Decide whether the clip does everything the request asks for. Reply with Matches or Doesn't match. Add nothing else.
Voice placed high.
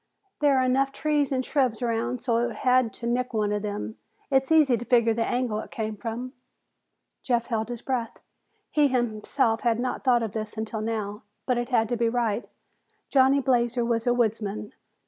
Matches